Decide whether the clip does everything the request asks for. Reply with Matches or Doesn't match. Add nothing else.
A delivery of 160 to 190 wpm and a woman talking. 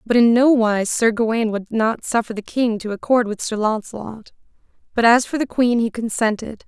Doesn't match